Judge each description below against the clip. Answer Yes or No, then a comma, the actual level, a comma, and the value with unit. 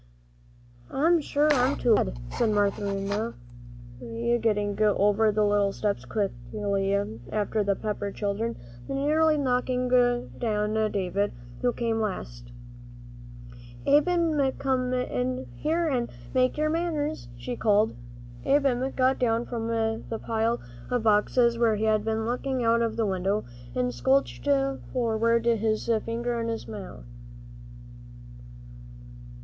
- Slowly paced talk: Yes, slow, 120 wpm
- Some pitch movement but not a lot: Yes, average, 3.6 semitones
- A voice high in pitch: Yes, high, 225 Hz